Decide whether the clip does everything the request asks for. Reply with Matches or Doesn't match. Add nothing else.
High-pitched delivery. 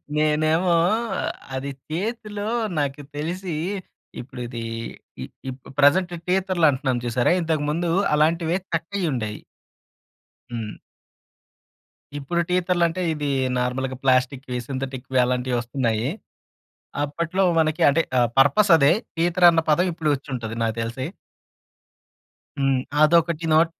Doesn't match